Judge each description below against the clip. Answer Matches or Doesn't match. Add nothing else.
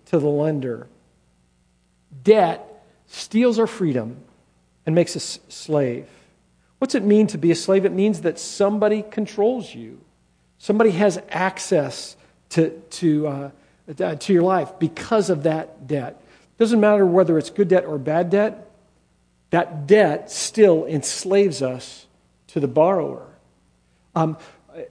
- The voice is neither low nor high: Matches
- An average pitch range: Doesn't match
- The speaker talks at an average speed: Doesn't match